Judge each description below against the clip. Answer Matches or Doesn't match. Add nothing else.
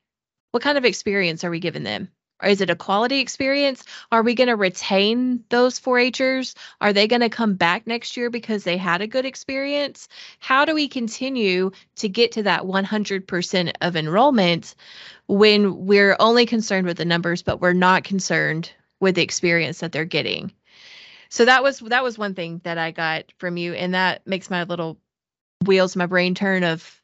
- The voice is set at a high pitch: Matches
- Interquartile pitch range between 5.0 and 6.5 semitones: Matches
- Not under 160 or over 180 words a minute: Doesn't match